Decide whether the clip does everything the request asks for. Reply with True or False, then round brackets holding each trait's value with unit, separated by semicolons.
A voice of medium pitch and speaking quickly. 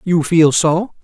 False (165 Hz; 175 wpm)